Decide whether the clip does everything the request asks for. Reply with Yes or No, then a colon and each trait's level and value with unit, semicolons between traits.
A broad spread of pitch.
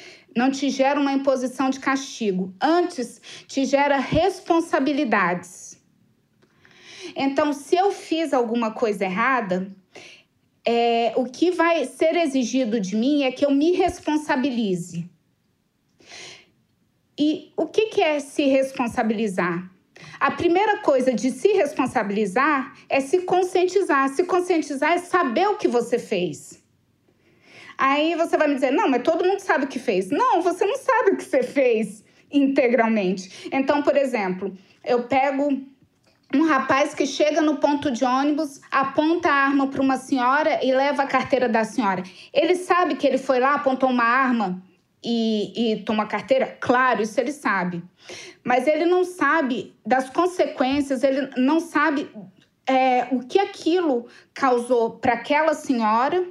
No: average, 4.7 semitones